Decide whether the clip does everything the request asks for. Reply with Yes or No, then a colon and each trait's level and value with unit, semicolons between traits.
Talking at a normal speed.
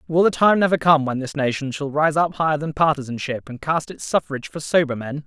No: fast, 240 wpm